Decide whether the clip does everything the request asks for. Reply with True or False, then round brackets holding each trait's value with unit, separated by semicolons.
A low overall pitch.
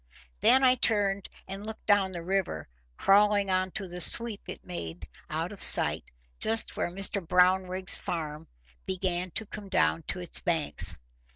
False (190 Hz)